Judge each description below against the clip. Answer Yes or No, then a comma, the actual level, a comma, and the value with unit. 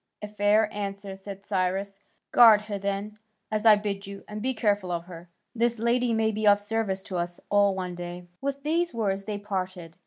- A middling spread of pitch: No, narrow, 2.2 semitones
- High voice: Yes, high, 205 Hz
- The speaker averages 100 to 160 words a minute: No, average, 195 wpm